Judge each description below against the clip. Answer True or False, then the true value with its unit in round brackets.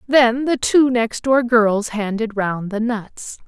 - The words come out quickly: False (175 wpm)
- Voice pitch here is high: True (230 Hz)